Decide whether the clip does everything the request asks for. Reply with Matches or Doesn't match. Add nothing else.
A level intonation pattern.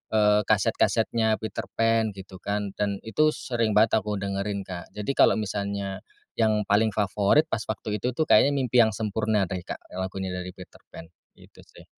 Matches